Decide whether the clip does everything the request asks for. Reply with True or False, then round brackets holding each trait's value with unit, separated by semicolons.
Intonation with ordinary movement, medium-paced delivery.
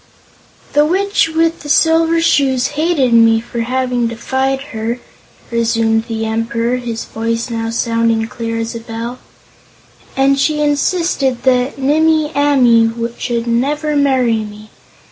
False (4.1 semitones; 130 wpm)